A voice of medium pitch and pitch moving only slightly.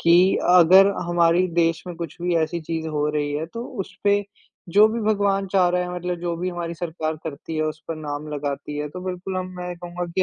Yes: medium, 175 Hz; narrow, 2.3 semitones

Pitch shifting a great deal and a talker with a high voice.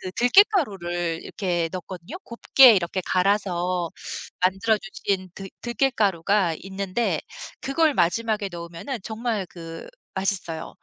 No: average, 4.3 semitones; high, 195 Hz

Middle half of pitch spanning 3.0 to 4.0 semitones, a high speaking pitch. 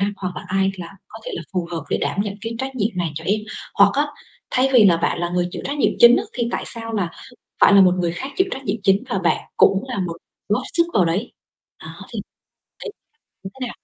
No: average, 4.9 semitones; high, 200 Hz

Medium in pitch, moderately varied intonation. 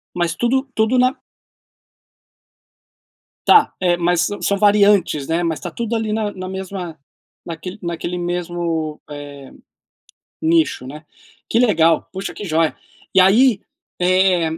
Yes: medium, 180 Hz; average, 4.0 semitones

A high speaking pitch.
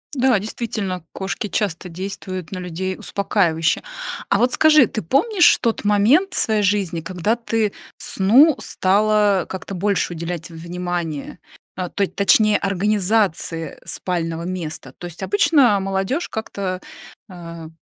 Yes: high, 195 Hz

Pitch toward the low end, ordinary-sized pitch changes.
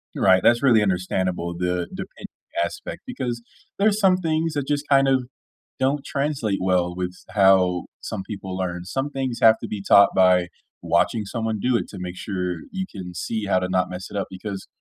No: low, 100 Hz; wide, 6.2 semitones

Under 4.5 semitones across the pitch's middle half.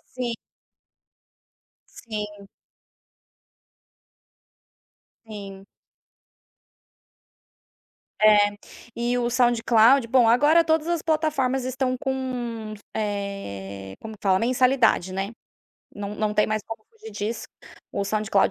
Yes: average, 3.9 semitones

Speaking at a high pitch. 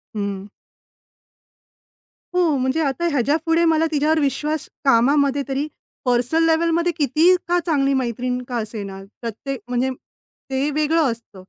Yes: very high, 275 Hz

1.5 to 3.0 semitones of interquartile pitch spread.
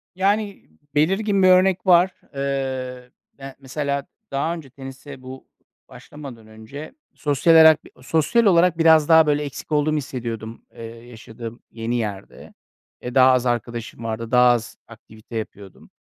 No: average, 5.1 semitones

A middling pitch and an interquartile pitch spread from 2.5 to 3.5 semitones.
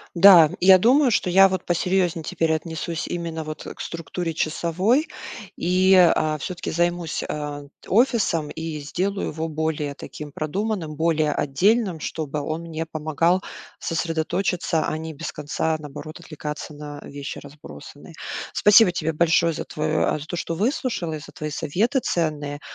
Yes: medium, 160 Hz; average, 2.9 semitones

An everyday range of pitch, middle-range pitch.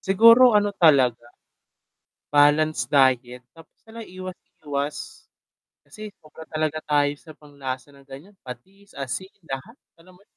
No: wide, 5.7 semitones; medium, 150 Hz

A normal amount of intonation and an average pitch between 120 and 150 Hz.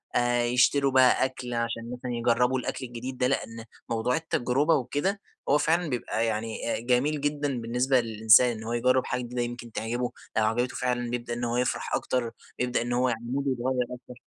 No: narrow, 1.6 semitones; low, 125 Hz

